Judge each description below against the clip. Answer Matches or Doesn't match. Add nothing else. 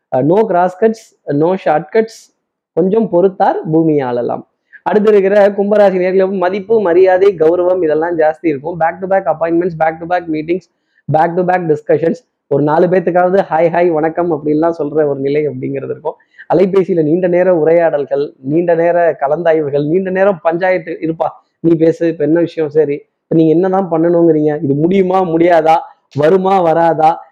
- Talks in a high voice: Doesn't match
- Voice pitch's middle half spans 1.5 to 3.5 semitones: Matches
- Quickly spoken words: Matches